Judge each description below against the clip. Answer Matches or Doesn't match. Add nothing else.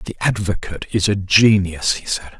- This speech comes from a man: Matches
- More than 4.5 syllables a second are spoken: Matches